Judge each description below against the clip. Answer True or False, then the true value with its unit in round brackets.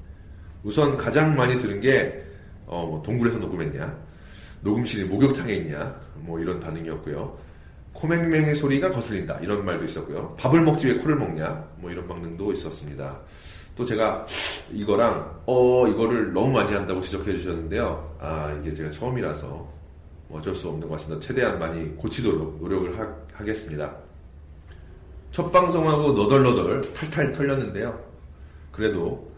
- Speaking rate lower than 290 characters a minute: False (320 characters per minute)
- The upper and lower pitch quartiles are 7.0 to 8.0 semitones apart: True (7.6 semitones)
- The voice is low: True (90 Hz)